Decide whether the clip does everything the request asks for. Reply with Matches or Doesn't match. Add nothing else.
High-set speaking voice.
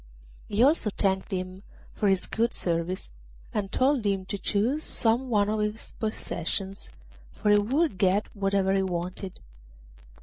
Matches